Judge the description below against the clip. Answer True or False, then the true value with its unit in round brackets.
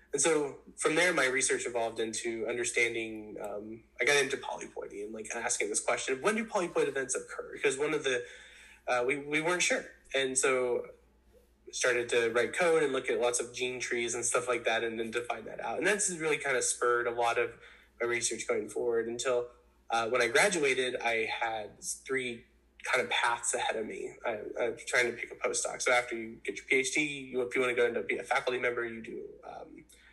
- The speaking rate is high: True (220 wpm)